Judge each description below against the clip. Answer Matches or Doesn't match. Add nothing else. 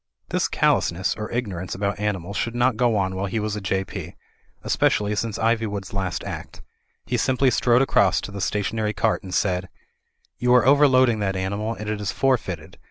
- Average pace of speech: Matches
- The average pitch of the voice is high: Doesn't match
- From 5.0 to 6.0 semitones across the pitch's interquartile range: Doesn't match